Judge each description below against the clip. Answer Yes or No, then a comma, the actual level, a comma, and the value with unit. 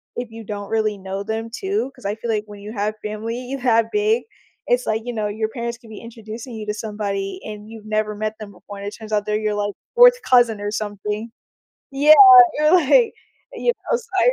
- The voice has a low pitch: No, high, 220 Hz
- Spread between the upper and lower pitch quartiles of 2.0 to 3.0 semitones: Yes, average, 2.7 semitones